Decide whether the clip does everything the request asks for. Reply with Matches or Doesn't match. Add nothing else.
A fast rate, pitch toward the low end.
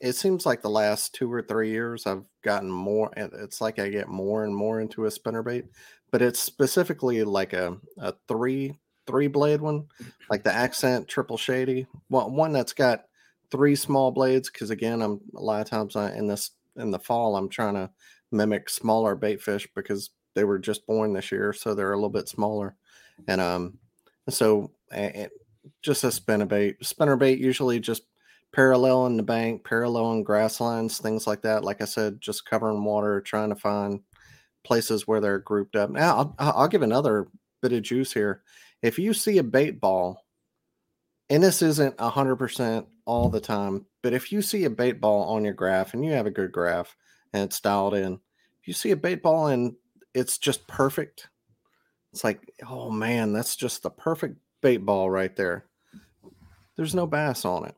Doesn't match